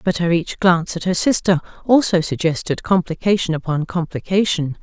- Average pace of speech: Yes, average, 150 wpm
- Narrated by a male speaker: No, female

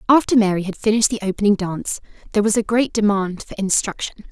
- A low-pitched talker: No, high, 210 Hz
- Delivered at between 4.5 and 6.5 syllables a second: No, 7.0 syllables/s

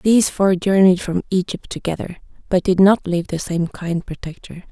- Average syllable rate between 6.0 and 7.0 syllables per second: No, 5.3 syllables/s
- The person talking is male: No, female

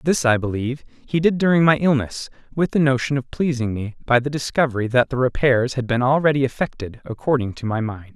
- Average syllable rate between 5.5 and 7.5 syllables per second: Yes, 5.9 syllables/s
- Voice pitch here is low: Yes, low, 130 Hz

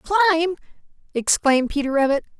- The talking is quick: No, slow, 100 wpm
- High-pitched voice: Yes, very high, 310 Hz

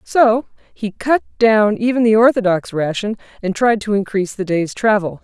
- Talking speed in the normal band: Yes, average, 170 wpm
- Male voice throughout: No, female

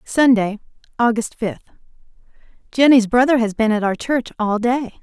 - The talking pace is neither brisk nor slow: No, slow, 130 wpm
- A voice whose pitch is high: Yes, high, 235 Hz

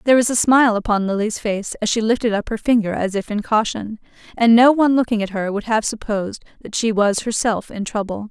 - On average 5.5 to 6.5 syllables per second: Yes, 6.0 syllables/s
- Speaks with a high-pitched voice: Yes, high, 220 Hz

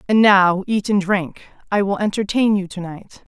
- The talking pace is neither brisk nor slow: Yes, average, 195 wpm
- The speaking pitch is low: No, high, 200 Hz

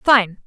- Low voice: No, high, 220 Hz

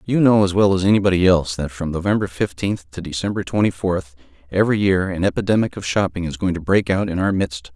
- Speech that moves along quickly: Yes, fast, 225 wpm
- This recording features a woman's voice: No, male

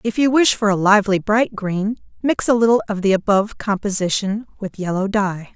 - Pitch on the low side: No, high, 205 Hz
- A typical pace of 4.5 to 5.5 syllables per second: Yes, 5.4 syllables/s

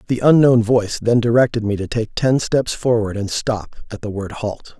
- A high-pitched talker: No, low, 115 Hz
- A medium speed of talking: No, fast, 215 wpm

